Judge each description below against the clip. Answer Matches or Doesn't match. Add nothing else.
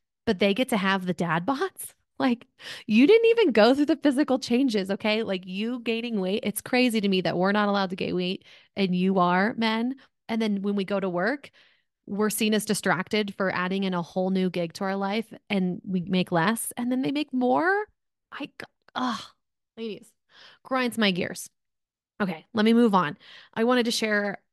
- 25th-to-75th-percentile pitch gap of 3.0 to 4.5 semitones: Matches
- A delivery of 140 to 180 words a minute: Doesn't match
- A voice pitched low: Doesn't match